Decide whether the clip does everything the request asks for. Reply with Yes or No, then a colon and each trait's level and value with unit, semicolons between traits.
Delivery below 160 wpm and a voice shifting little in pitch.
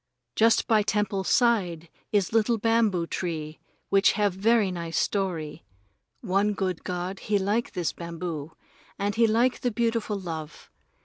No: average, 140 wpm; average, 4.1 semitones